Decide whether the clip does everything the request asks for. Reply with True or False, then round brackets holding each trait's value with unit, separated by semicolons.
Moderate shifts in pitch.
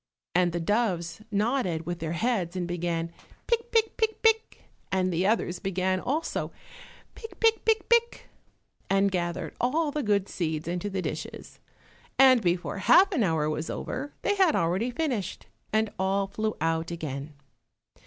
False (7.5 semitones)